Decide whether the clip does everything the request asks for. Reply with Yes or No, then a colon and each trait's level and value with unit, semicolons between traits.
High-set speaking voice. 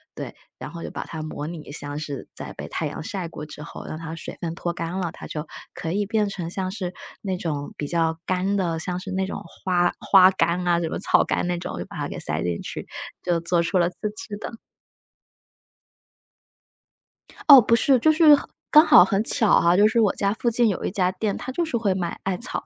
No: medium, 180 Hz